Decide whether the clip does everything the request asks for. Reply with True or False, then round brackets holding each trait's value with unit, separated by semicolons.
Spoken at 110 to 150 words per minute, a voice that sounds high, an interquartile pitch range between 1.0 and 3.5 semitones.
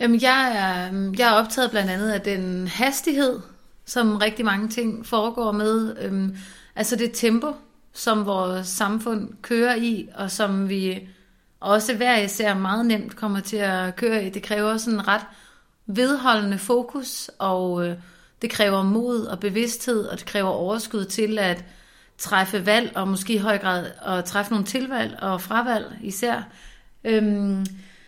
True (145 wpm; 215 Hz; 3.1 semitones)